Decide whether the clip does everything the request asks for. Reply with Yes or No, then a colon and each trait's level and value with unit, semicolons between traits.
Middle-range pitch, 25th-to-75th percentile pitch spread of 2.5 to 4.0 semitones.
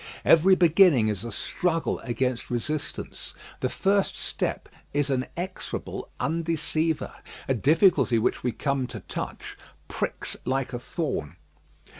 No: medium, 145 Hz; average, 4.8 semitones